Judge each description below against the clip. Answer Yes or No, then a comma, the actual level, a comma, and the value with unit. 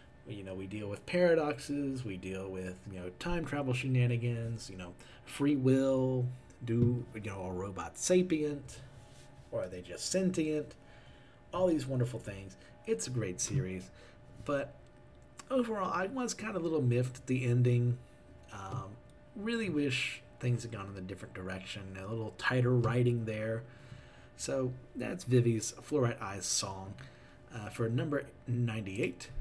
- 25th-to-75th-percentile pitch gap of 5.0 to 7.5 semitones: Yes, wide, 5.4 semitones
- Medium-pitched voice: No, low, 120 Hz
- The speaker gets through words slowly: No, average, 150 wpm